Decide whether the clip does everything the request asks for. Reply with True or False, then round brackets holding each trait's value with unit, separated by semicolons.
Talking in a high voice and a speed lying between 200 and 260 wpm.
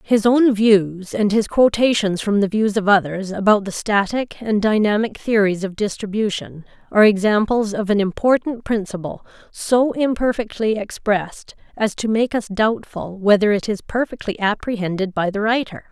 False (210 Hz; 155 wpm)